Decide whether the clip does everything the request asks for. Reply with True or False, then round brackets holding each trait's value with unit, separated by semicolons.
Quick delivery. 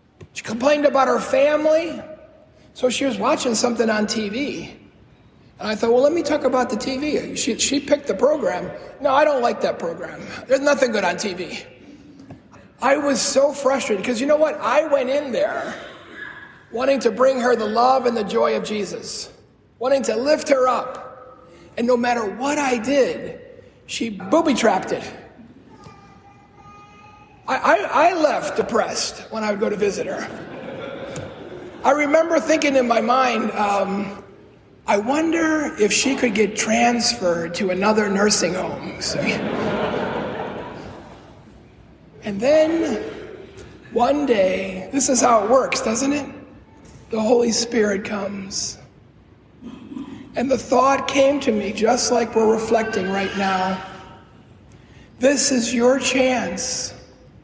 False (140 wpm)